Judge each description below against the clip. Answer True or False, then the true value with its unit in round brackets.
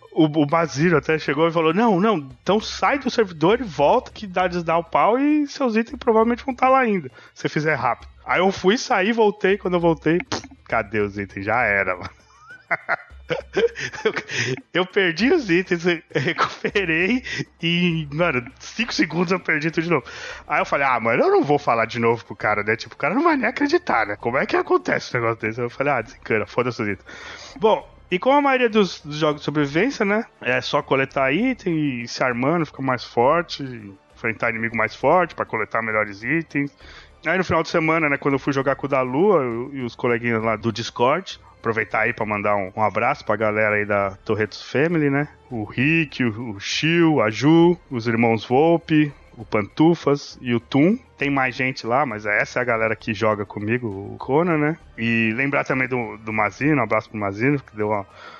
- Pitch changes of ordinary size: False (7.7 semitones)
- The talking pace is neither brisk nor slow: False (205 wpm)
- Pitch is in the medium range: True (145 Hz)